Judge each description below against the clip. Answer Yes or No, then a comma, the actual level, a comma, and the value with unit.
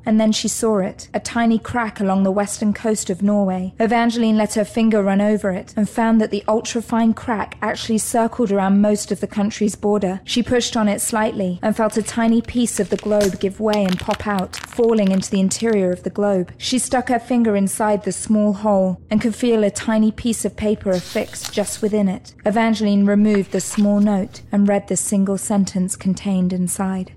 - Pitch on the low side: No, high, 210 Hz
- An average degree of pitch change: No, narrow, 2.1 semitones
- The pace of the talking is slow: No, fast, 205 wpm